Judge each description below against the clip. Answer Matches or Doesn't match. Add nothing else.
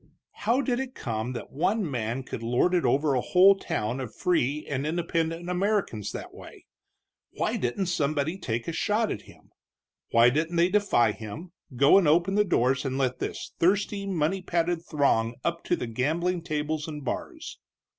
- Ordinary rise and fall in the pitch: Doesn't match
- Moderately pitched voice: Matches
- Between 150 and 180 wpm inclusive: Matches